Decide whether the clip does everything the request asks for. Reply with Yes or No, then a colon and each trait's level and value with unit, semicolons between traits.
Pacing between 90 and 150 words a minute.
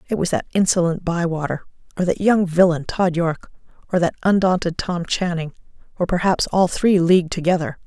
Yes: average, 145 wpm